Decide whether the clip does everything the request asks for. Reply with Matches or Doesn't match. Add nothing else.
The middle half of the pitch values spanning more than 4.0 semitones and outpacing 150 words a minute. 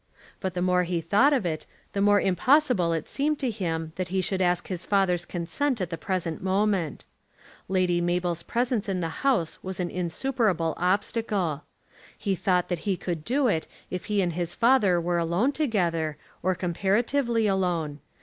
Doesn't match